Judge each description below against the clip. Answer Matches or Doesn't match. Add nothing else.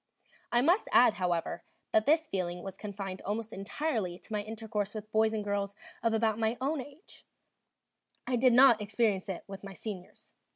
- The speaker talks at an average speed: Matches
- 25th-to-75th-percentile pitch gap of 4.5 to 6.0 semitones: Doesn't match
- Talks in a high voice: Matches